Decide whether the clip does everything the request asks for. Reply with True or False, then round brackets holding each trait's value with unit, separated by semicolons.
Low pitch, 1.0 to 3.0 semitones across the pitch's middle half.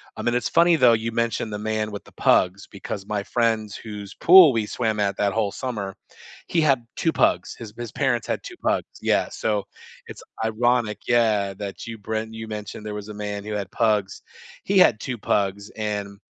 True (110 Hz; 2.4 semitones)